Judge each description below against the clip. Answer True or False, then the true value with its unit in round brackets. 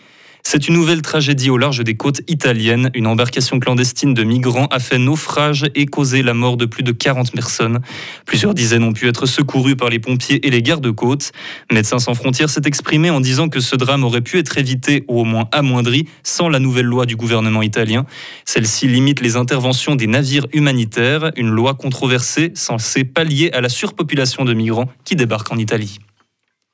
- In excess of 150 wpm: True (190 wpm)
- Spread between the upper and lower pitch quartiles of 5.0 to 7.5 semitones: False (3.3 semitones)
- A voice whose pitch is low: True (130 Hz)